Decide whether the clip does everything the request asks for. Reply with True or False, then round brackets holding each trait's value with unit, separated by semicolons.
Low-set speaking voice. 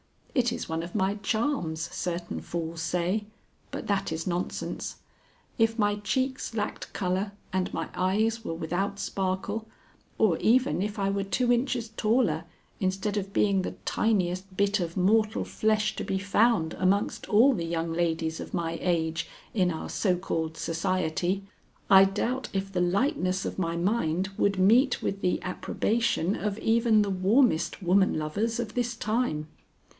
False (195 Hz)